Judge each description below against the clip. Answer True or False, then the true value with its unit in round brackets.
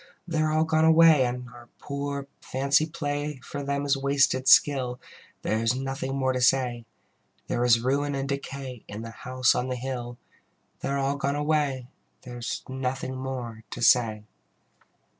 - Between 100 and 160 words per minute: False (170 wpm)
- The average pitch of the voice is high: False (135 Hz)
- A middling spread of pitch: False (2.3 semitones)